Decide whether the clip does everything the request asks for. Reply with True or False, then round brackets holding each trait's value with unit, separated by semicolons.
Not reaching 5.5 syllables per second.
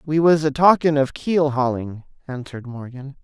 True (5.0 syllables/s)